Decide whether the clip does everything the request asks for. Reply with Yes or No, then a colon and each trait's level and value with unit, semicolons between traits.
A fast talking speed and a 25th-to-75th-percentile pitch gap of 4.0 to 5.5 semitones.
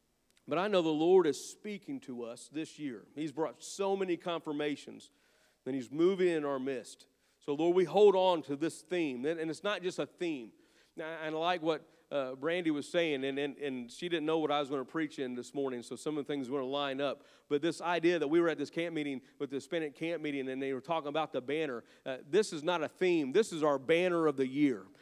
No: fast, 240 wpm; average, 3.3 semitones